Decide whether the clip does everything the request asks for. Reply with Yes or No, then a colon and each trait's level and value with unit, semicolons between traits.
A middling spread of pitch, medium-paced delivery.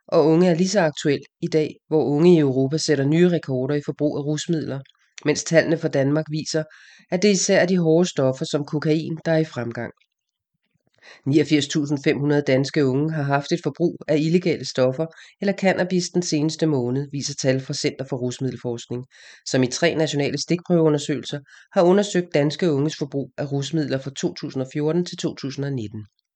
Yes: average, 3.0 semitones; average, 170 wpm